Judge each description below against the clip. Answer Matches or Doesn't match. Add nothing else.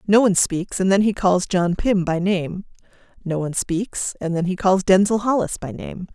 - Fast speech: Matches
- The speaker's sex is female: Matches